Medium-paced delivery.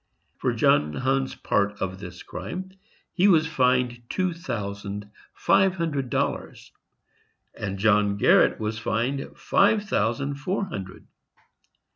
No: slow, 120 wpm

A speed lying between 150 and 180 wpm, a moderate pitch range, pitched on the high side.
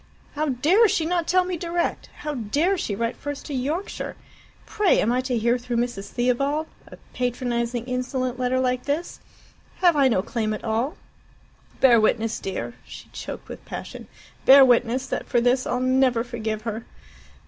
Yes: average, 170 wpm; average, 3.5 semitones; very high, 250 Hz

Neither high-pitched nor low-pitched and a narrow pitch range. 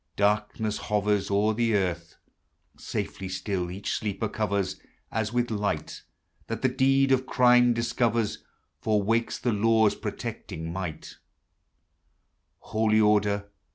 No: low, 105 Hz; narrow, 2.2 semitones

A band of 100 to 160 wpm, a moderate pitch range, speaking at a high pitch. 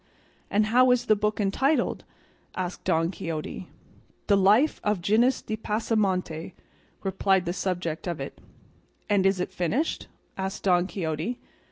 Yes: average, 140 wpm; average, 3.5 semitones; high, 195 Hz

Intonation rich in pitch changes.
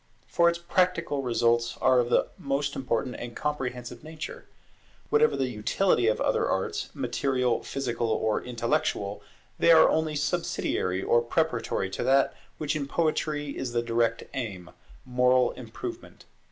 No: average, 4.1 semitones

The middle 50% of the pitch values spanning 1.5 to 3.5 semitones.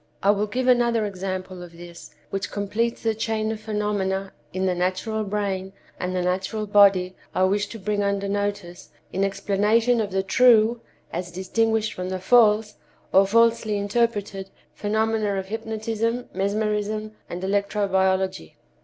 Yes: narrow, 2.4 semitones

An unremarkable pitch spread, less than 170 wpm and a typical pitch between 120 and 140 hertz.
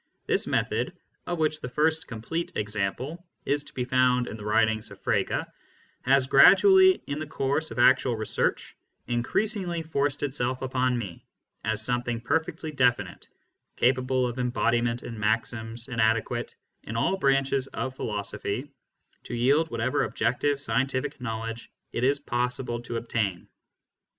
Yes: average, 3.5 semitones; average, 140 wpm; low, 125 Hz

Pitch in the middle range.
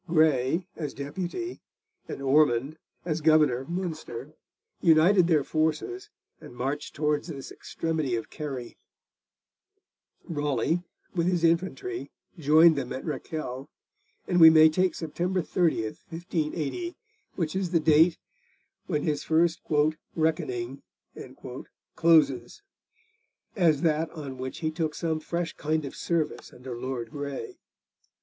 Yes: medium, 155 Hz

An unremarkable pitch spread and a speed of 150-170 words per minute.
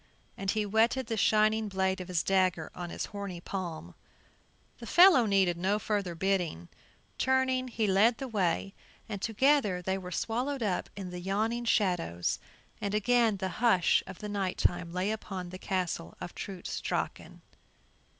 Yes: average, 3.4 semitones; average, 160 wpm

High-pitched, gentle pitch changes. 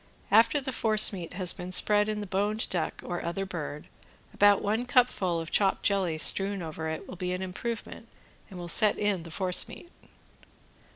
No: high, 195 Hz; average, 3.2 semitones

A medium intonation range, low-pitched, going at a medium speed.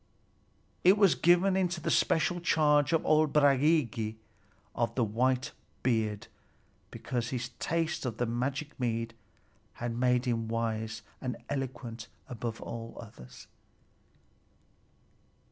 No: average, 4.8 semitones; low, 125 Hz; slow, 115 wpm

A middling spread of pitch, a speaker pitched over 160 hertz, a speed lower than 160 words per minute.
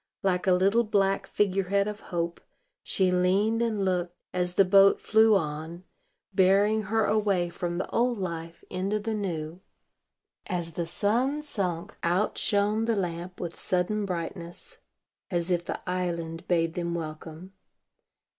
Yes: average, 3.1 semitones; medium, 185 Hz; average, 145 wpm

